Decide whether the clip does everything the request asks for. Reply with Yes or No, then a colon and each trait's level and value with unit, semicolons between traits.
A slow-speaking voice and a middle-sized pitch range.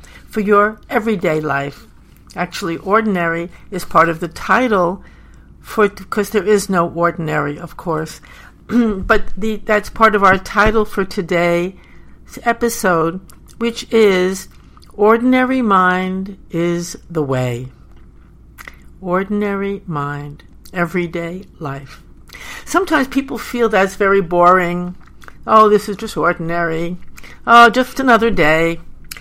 Yes: slow, 115 wpm; average, 4.2 semitones